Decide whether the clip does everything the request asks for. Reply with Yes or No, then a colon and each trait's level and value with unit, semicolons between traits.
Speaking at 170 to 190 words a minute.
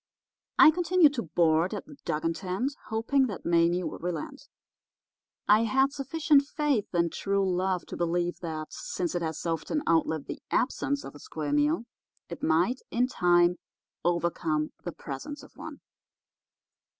No: average, 150 wpm